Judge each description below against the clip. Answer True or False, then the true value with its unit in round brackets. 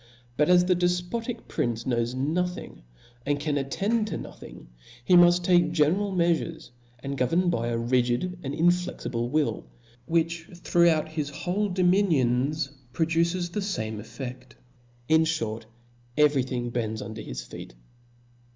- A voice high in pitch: False (160 Hz)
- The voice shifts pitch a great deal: True (6.2 semitones)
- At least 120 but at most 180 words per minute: True (140 wpm)